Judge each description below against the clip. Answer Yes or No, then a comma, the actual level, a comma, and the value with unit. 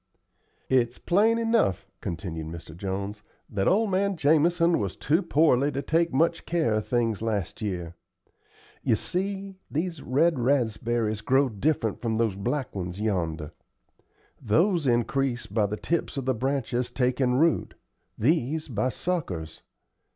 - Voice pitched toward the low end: Yes, low, 125 Hz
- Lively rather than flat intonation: Yes, wide, 7.5 semitones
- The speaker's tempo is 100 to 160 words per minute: Yes, slow, 135 wpm